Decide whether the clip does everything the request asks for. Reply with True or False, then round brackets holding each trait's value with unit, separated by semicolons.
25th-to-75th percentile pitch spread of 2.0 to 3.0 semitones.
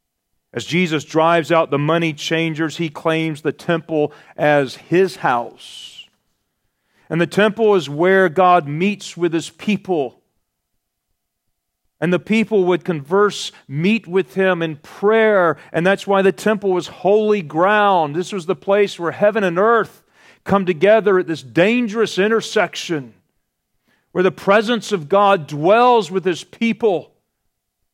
False (3.8 semitones)